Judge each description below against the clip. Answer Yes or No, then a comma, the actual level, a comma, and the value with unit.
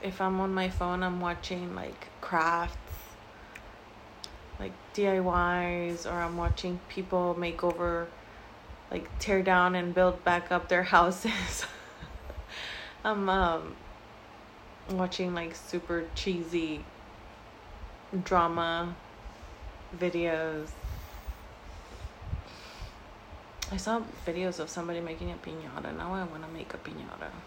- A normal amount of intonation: No, narrow, 1.4 semitones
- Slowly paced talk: Yes, slow, 105 wpm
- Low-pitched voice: No, medium, 175 Hz